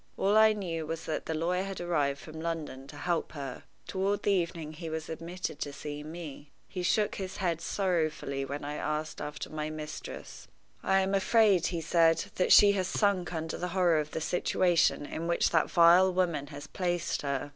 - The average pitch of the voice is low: No, medium, 170 Hz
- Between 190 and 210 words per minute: Yes, average, 195 wpm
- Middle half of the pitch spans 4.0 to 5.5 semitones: No, average, 3.3 semitones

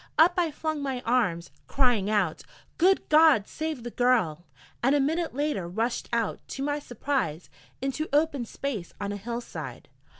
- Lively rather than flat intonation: Yes, wide, 5.8 semitones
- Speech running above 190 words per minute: No, average, 165 wpm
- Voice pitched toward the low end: No, very high, 255 Hz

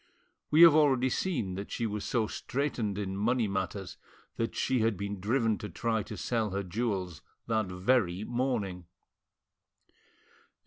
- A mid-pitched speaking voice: No, low, 110 Hz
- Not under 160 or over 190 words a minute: No, average, 145 wpm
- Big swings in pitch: No, average, 4.0 semitones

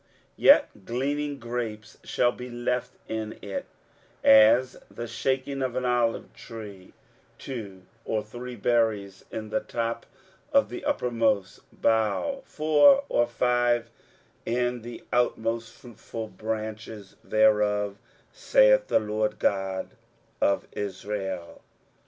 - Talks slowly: Yes, slow, 115 wpm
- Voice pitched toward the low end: Yes, low, 115 Hz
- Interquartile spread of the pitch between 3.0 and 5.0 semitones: No, narrow, 2.6 semitones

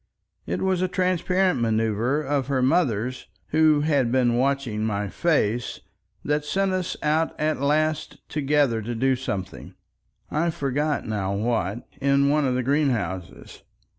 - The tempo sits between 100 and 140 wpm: Yes, slow, 135 wpm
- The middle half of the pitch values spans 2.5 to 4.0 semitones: No, average, 4.7 semitones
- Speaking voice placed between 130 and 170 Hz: Yes, medium, 140 Hz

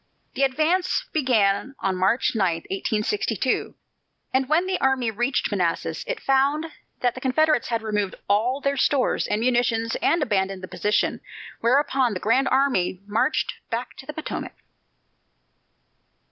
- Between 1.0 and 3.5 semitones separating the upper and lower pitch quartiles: No, average, 4.9 semitones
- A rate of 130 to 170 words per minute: Yes, average, 140 wpm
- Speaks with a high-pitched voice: Yes, very high, 250 Hz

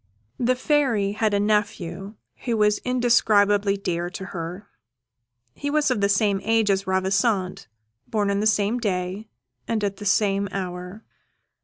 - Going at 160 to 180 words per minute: No, average, 150 wpm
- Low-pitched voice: No, high, 205 Hz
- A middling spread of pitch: No, narrow, 2.3 semitones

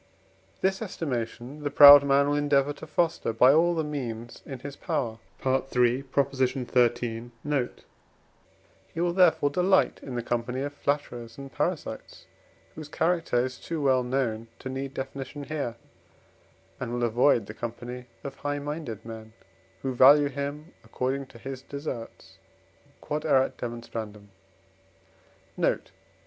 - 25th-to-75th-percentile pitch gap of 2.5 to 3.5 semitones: Yes, average, 3.2 semitones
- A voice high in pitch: No, low, 135 Hz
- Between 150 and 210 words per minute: No, slow, 135 wpm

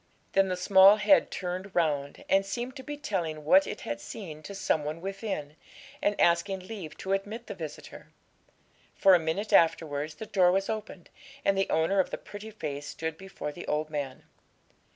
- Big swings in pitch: No, average, 4.1 semitones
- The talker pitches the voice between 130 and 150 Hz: No, medium, 185 Hz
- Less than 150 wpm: No, average, 185 wpm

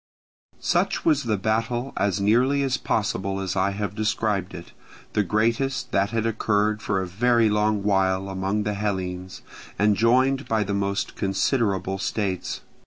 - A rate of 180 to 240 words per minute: No, average, 155 wpm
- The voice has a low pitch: Yes, low, 105 Hz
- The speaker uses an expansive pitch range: No, average, 2.8 semitones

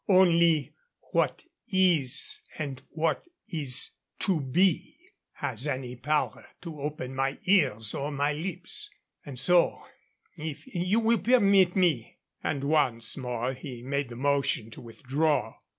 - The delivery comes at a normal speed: No, slow, 130 wpm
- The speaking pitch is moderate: Yes, medium, 145 Hz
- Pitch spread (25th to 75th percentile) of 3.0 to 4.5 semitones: No, average, 4.9 semitones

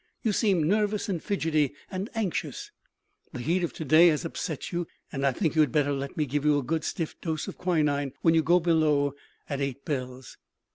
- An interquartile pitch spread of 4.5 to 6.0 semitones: No, average, 3.4 semitones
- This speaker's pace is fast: Yes, fast, 210 wpm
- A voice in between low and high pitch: Yes, medium, 155 Hz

